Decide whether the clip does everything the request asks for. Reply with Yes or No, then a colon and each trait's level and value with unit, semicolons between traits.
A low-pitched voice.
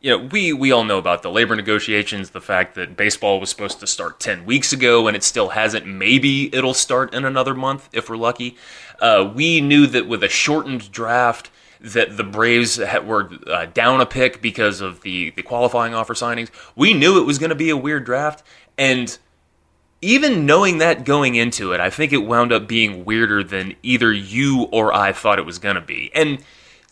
Yes: low, 120 Hz